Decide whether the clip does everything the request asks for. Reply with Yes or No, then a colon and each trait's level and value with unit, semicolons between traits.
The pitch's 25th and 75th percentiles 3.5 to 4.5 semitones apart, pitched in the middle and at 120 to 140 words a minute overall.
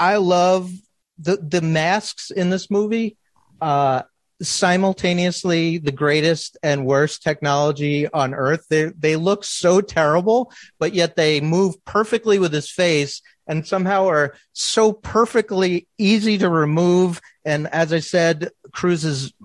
Yes: average, 4.0 semitones; medium, 175 Hz; slow, 135 wpm